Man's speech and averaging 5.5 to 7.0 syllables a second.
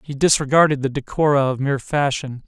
Yes: male; 6.0 syllables/s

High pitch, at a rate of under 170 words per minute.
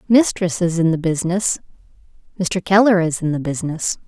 No: medium, 175 Hz; average, 160 wpm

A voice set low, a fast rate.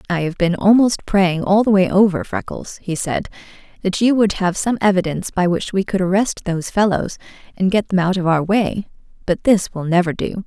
No: high, 190 Hz; fast, 210 wpm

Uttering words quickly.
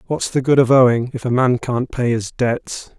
Yes: fast, 240 wpm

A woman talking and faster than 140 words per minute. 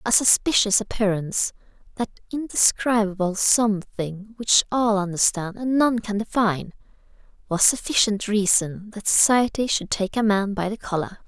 No: female; slow, 135 wpm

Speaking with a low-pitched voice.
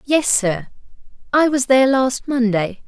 No: high, 245 Hz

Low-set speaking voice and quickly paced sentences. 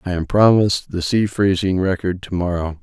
No: very low, 90 Hz; average, 190 wpm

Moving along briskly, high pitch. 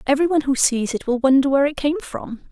Yes: fast, 265 wpm; very high, 275 Hz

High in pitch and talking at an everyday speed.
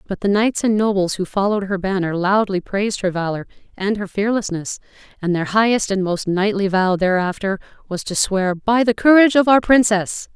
Yes: high, 200 Hz; average, 190 wpm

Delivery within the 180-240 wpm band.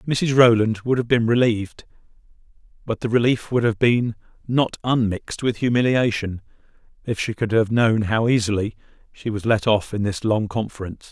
No: average, 165 wpm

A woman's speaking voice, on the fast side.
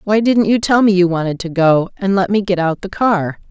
Yes: female; fast, 275 wpm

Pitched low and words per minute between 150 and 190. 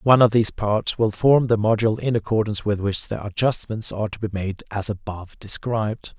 No: low, 105 Hz; fast, 205 wpm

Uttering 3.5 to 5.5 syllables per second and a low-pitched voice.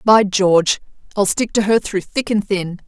No: 4.6 syllables/s; high, 200 Hz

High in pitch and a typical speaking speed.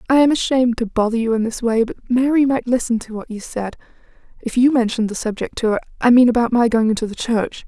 No: high, 235 Hz; fast, 240 wpm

